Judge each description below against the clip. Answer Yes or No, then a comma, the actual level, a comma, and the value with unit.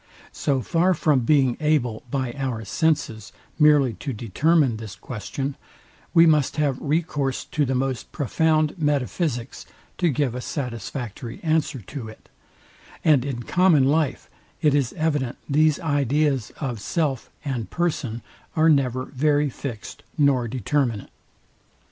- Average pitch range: Yes, average, 3.8 semitones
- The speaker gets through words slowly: Yes, slow, 130 wpm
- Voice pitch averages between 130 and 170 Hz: Yes, medium, 140 Hz